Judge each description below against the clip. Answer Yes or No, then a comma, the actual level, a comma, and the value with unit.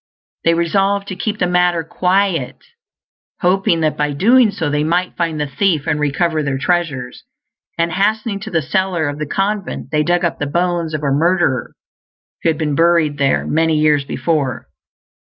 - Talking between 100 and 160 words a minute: No, average, 175 wpm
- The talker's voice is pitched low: No, medium, 165 Hz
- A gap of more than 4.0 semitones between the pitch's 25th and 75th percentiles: No, average, 3.5 semitones